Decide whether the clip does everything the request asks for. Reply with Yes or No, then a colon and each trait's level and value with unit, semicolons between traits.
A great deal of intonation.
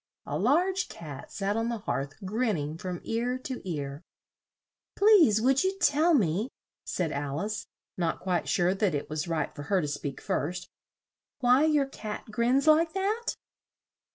Yes: wide, 8.8 semitones